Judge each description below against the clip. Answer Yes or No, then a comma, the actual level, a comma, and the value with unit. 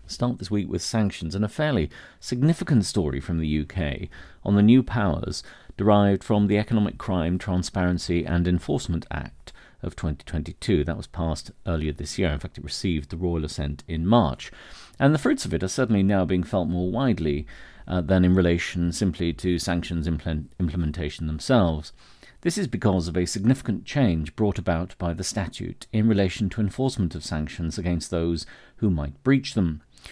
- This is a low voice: Yes, very low, 90 Hz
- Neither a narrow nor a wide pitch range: Yes, average, 4.2 semitones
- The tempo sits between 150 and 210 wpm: Yes, average, 175 wpm